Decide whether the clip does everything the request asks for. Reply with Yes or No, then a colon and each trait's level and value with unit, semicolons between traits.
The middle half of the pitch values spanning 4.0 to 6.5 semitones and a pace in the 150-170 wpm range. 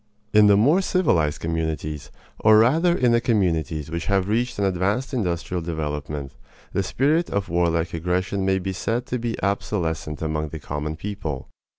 Yes: average, 5.3 semitones; average, 165 wpm